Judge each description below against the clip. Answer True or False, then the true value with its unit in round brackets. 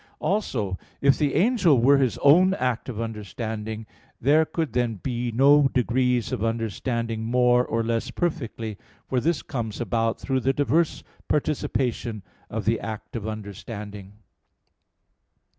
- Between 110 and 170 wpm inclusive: True (135 wpm)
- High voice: False (120 Hz)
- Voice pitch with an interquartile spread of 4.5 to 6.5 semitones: False (3.7 semitones)